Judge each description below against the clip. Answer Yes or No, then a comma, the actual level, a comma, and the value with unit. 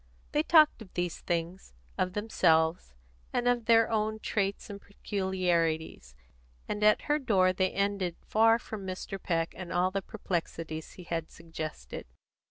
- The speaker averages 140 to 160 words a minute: Yes, average, 150 wpm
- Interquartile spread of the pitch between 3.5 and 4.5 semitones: Yes, average, 4.2 semitones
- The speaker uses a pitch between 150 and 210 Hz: Yes, medium, 185 Hz